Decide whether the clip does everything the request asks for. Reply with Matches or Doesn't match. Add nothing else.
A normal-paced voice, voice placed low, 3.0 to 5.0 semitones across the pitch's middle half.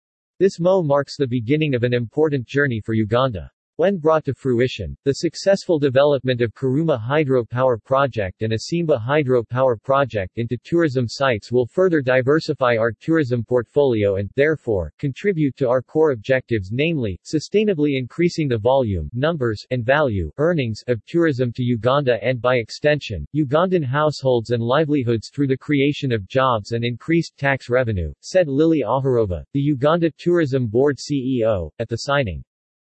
Matches